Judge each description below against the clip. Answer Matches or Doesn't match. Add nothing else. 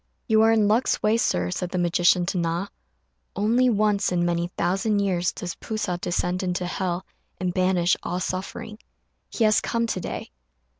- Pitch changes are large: Doesn't match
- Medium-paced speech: Matches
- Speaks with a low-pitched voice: Doesn't match